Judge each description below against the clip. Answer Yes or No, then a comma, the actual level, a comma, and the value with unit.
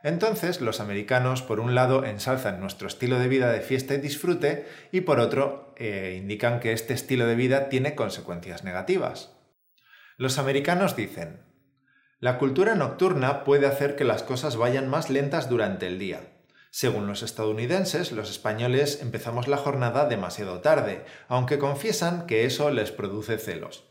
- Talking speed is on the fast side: No, average, 155 wpm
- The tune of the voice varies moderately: Yes, average, 3.6 semitones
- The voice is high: No, low, 130 Hz